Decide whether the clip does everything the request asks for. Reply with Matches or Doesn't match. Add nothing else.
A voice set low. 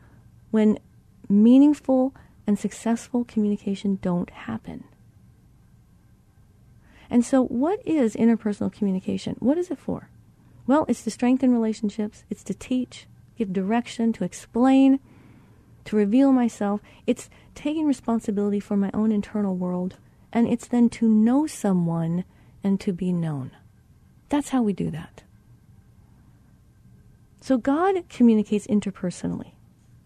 Doesn't match